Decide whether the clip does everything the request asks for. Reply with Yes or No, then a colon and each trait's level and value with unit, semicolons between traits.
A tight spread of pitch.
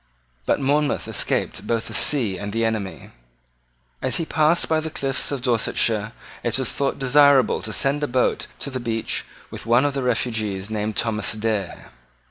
No: average, 4.3 semitones